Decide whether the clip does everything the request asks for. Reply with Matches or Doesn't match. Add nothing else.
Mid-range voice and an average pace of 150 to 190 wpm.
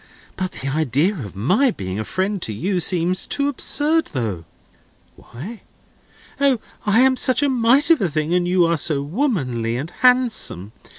Matches